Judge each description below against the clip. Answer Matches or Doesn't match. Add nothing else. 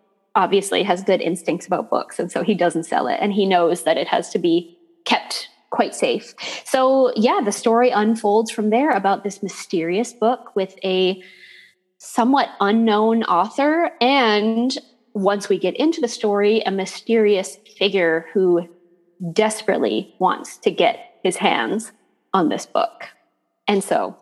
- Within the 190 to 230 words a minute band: Doesn't match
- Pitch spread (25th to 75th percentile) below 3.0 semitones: Doesn't match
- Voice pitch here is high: Matches